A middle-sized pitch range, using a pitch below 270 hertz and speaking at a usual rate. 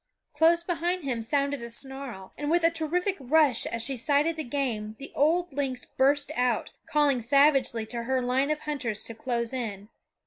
No: average, 4.2 semitones; very high, 275 Hz; average, 180 wpm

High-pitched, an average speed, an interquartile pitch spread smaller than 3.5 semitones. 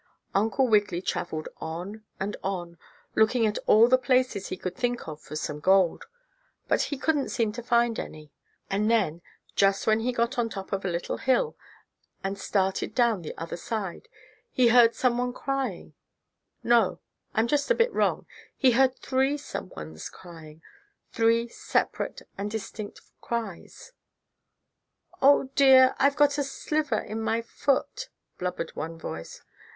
No: high, 225 Hz; average, 155 wpm; wide, 5.4 semitones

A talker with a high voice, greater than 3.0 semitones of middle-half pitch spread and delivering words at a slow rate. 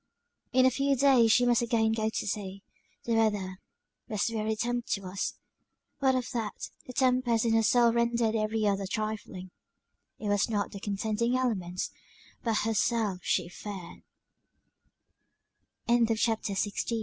No: high, 220 Hz; narrow, 2.6 semitones; slow, 125 wpm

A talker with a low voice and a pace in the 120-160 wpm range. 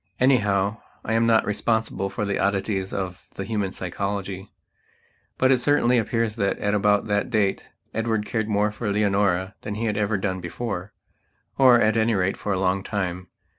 No: low, 105 Hz; average, 170 wpm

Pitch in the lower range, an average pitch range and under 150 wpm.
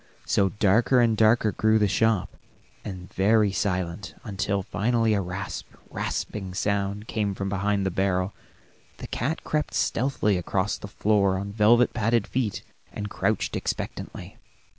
No: low, 100 Hz; narrow, 2.3 semitones; average, 140 wpm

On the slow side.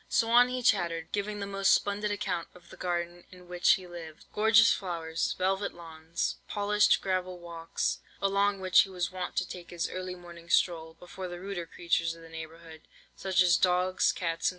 No: average, 190 wpm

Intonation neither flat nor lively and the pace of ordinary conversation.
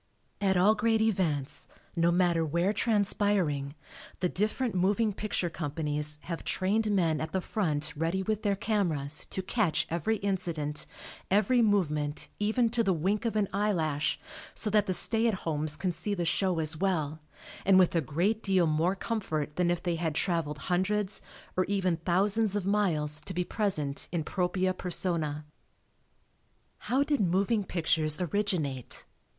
Yes: average, 4.5 semitones; average, 155 wpm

